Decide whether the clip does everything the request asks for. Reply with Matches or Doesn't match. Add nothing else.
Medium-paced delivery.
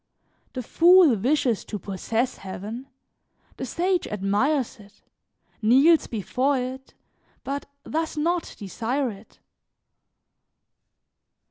Doesn't match